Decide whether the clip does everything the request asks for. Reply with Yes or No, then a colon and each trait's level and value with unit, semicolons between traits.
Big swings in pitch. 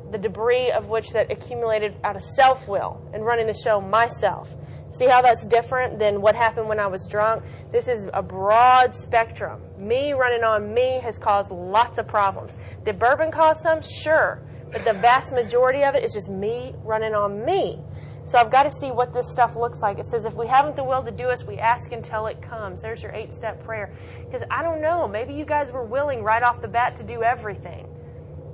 No: average, 3.1 semitones